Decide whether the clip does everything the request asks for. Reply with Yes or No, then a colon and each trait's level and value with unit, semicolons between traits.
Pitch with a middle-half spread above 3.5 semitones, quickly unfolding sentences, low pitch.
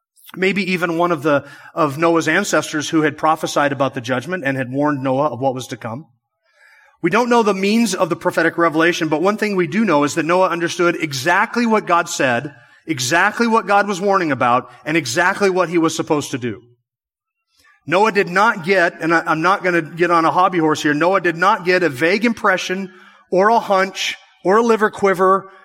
No: average, 4.2 semitones; fast, 210 wpm; medium, 175 Hz